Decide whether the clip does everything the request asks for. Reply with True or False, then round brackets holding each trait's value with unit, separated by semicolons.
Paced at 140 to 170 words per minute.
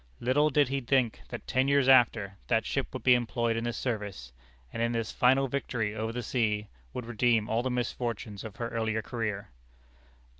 False (190 wpm)